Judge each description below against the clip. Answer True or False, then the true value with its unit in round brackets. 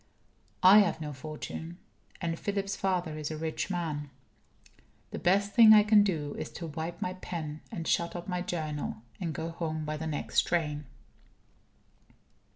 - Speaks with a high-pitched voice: False (165 Hz)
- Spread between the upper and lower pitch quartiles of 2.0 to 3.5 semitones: True (3.1 semitones)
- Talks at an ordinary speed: True (165 wpm)